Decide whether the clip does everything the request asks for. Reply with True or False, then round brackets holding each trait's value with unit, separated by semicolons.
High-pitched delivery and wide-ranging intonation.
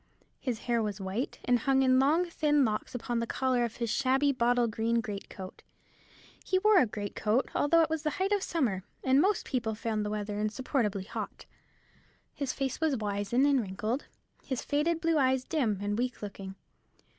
False (245 Hz; 5.0 semitones)